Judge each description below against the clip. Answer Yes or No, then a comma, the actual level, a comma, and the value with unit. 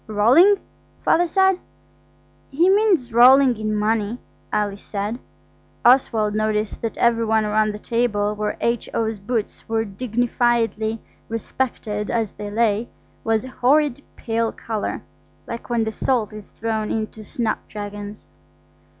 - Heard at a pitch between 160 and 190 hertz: No, high, 225 Hz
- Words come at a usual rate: No, slow, 125 wpm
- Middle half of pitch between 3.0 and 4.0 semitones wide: No, narrow, 2.4 semitones